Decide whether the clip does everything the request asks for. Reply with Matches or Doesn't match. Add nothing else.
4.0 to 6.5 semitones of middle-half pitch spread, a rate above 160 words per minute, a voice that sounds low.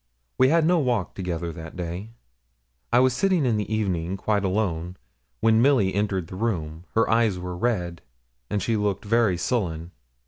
Matches